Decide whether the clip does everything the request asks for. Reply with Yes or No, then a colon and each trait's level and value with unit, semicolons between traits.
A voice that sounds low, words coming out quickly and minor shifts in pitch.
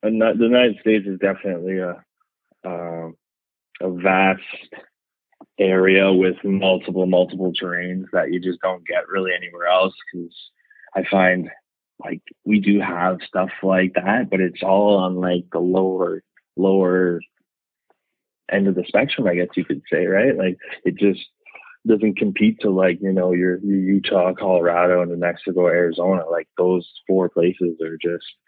No: very low, 95 Hz; average, 155 wpm; narrow, 1.4 semitones